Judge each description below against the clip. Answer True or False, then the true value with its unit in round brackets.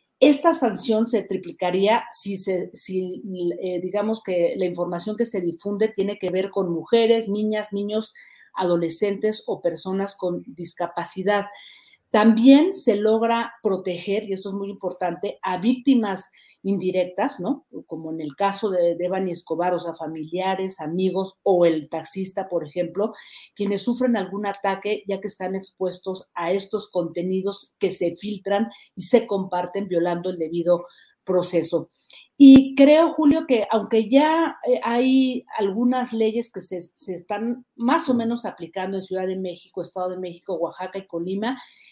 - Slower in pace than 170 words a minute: True (150 wpm)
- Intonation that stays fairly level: False (3.7 semitones)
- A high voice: True (195 Hz)